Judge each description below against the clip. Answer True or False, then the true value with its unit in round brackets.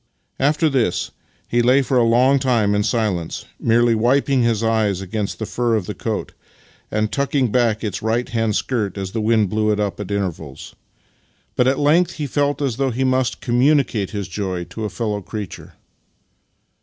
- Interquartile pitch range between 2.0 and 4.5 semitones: True (3.8 semitones)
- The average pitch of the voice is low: True (115 Hz)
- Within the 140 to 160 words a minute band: False (180 wpm)